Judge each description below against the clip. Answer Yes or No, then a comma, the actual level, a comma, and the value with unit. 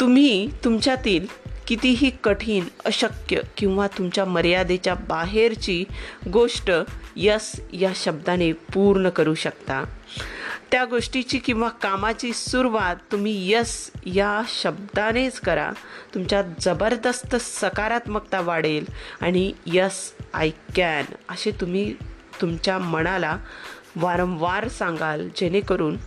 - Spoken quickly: No, average, 95 wpm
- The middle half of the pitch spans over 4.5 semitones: No, average, 4.2 semitones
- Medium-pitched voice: No, high, 200 Hz